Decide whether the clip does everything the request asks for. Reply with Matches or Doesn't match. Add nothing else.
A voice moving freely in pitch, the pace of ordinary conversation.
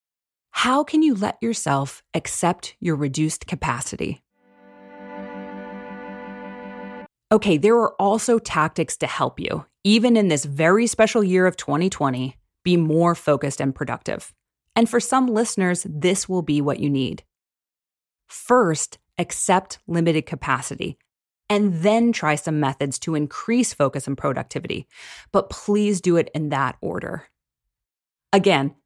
Doesn't match